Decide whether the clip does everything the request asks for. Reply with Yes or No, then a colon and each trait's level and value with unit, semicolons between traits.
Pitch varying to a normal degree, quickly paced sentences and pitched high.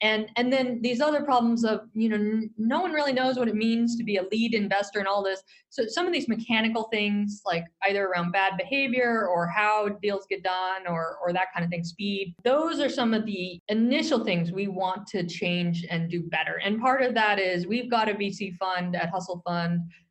Yes: average, 3.9 semitones; fast, 225 wpm; high, 205 Hz